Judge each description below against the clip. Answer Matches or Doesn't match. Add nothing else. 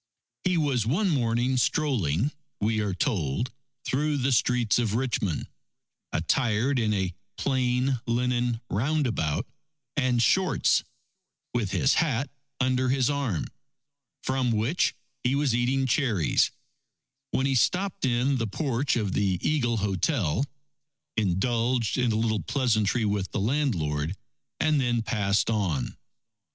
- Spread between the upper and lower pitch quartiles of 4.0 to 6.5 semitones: Matches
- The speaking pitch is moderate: Doesn't match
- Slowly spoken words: Matches